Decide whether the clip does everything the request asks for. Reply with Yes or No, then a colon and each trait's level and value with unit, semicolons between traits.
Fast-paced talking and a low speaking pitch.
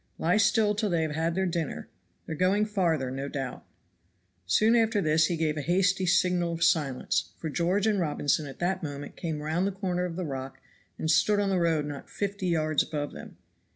No: fast, 210 wpm; medium, 170 Hz